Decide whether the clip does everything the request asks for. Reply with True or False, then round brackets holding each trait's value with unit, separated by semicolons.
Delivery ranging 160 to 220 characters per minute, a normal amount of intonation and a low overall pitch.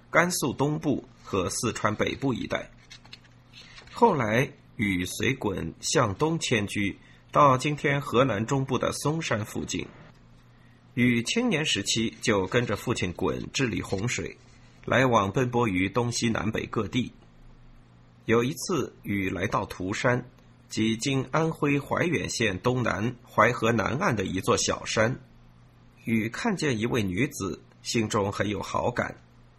True (195 characters per minute; 4.8 semitones; 120 Hz)